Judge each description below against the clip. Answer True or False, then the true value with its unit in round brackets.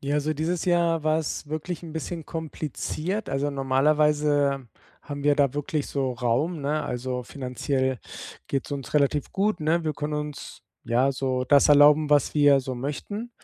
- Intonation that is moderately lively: False (2.3 semitones)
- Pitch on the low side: False (145 Hz)